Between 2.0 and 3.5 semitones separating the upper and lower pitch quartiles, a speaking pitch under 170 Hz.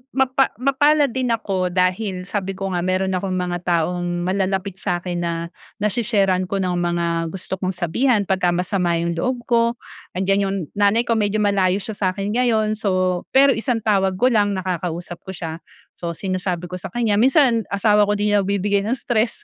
No: average, 3.2 semitones; high, 195 Hz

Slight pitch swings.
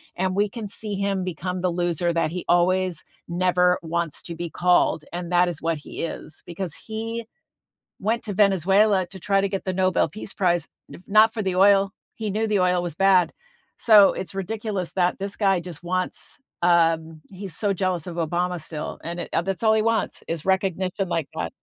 Yes: narrow, 2.3 semitones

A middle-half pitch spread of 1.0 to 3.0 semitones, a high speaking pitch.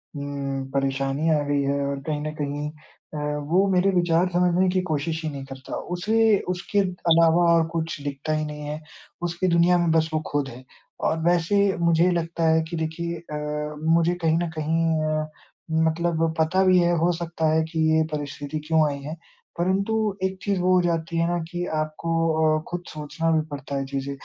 No: average, 2.7 semitones; medium, 160 Hz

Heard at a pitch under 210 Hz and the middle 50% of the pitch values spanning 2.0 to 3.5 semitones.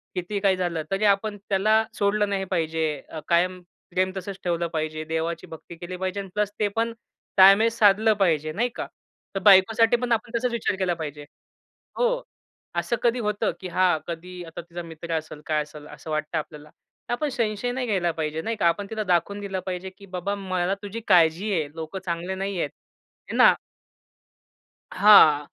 No: medium, 185 Hz; average, 4.0 semitones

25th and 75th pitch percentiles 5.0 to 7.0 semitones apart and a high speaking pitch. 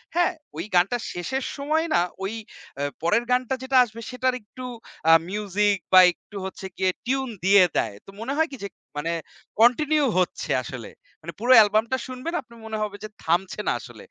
Yes: average, 5.3 semitones; high, 220 Hz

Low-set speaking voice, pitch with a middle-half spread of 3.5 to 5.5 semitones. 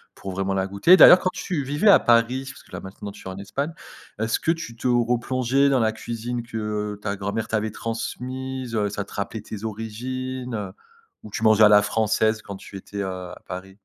Yes: low, 110 Hz; average, 3.8 semitones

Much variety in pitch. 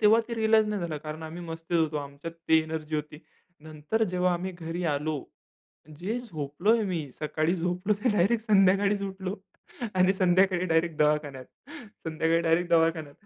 No: average, 3.7 semitones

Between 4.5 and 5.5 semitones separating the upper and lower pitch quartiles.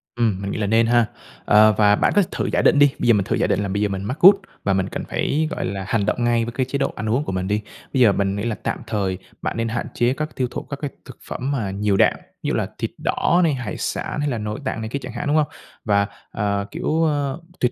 Yes: average, 4.9 semitones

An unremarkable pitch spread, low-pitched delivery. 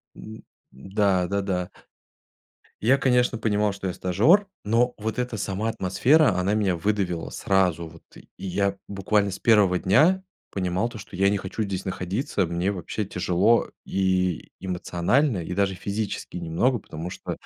Yes: average, 3.3 semitones; low, 100 Hz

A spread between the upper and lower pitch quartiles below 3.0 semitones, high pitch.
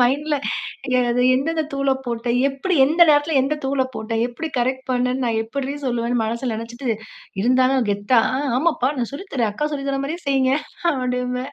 Yes: narrow, 2.6 semitones; very high, 260 Hz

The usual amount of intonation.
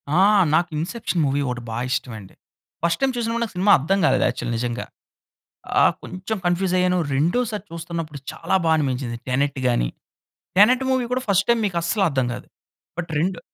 No: wide, 6.7 semitones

